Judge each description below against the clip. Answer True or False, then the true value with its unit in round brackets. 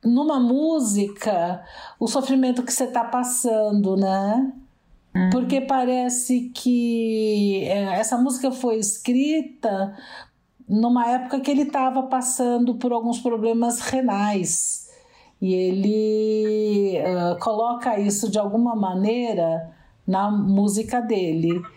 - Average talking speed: False (100 wpm)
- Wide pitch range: False (3.9 semitones)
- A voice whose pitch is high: True (230 Hz)